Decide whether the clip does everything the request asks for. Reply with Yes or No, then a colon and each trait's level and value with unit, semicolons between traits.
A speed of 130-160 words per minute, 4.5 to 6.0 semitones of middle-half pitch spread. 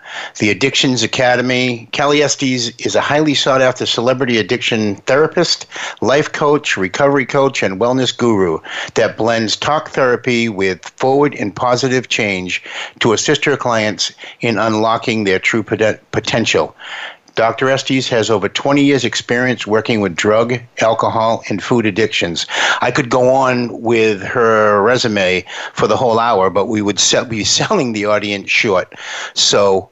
No: average, 145 wpm; average, 3.2 semitones